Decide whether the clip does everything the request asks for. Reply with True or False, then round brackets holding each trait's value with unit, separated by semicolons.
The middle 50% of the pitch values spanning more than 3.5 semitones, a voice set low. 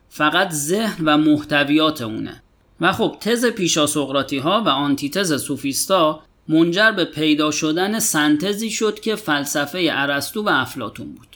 False (4.8 semitones; 155 Hz)